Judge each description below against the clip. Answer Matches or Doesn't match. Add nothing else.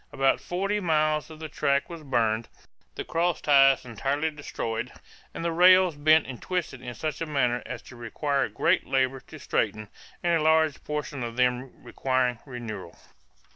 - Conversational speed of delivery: Matches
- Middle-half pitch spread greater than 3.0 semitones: Matches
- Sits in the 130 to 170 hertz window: Matches